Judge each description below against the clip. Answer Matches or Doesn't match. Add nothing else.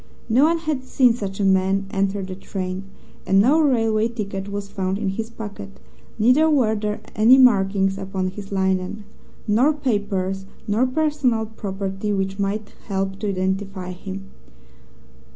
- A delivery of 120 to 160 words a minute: Matches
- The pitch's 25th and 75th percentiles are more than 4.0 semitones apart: Doesn't match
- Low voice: Doesn't match